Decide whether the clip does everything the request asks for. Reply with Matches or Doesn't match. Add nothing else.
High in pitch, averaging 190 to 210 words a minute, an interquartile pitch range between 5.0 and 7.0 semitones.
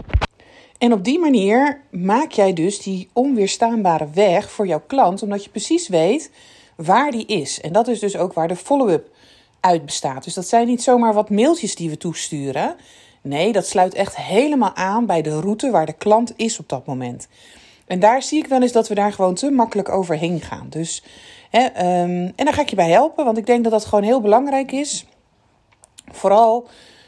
Matches